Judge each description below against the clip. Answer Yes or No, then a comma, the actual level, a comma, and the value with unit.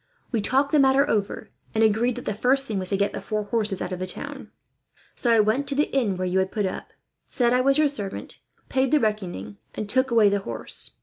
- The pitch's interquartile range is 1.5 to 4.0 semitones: No, average, 4.8 semitones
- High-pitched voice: Yes, high, 220 Hz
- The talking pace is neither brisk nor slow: No, fast, 245 wpm